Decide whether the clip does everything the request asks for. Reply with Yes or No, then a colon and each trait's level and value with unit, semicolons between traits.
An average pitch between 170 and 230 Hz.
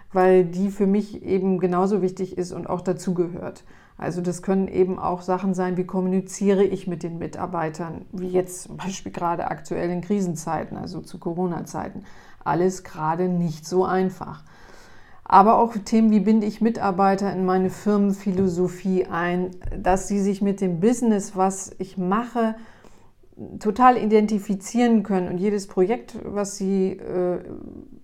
Yes: high, 190 Hz